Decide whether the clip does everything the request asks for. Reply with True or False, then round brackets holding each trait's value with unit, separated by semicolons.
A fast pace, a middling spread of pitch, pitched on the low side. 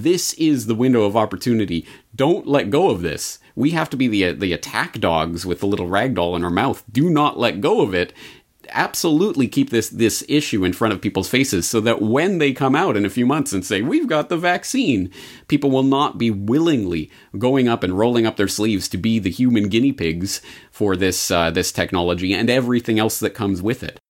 False (220 wpm; 5.8 semitones; 115 Hz)